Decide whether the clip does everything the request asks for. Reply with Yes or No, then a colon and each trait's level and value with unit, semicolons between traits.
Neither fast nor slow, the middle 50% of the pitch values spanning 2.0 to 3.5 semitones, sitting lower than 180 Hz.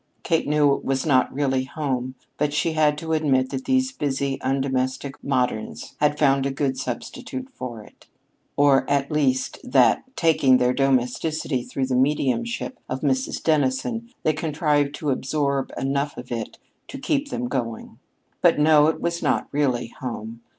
Yes: average, 160 wpm; average, 2.9 semitones; medium, 140 Hz